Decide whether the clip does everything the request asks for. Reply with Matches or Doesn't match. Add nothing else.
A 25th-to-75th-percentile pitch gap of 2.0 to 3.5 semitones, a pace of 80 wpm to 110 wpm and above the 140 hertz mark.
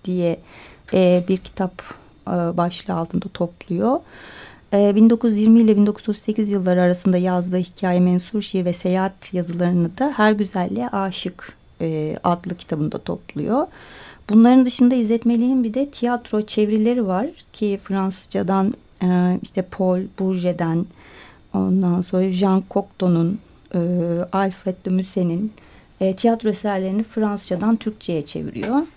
Matches